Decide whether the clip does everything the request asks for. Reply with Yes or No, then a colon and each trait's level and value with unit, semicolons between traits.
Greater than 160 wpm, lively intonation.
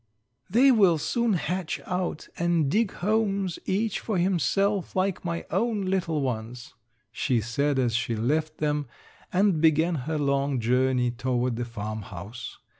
No: average, 140 wpm; wide, 7.2 semitones